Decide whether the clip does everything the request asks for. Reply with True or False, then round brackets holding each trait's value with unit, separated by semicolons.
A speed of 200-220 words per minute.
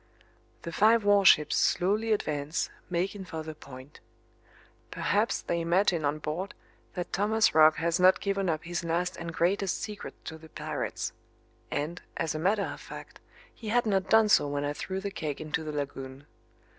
False (170 wpm)